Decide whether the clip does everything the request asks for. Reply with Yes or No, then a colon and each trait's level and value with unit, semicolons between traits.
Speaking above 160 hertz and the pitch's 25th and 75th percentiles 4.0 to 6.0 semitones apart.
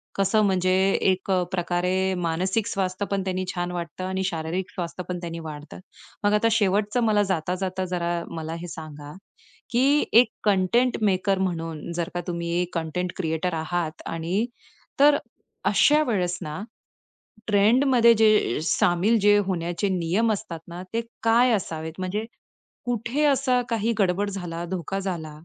No: medium, 185 Hz; average, 3.6 semitones